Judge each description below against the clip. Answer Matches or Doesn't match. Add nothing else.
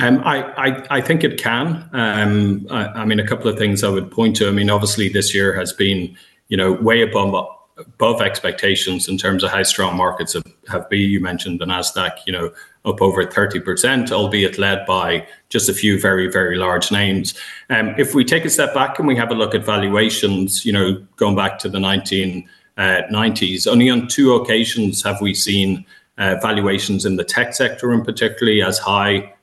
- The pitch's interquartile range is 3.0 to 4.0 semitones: Doesn't match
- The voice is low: Matches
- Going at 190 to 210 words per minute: Matches